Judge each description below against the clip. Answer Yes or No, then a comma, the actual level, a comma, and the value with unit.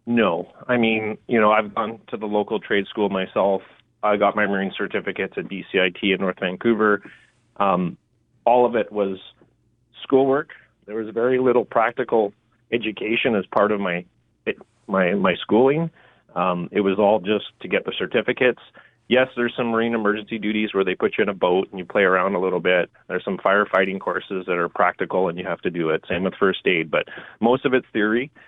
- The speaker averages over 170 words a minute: Yes, average, 200 wpm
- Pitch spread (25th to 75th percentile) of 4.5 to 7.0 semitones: No, average, 2.9 semitones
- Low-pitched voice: Yes, low, 110 Hz